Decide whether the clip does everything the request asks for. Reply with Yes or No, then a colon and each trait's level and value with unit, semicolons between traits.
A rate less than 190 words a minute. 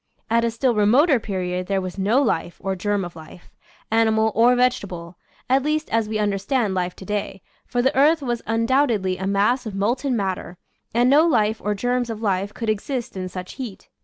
No: average, 200 wpm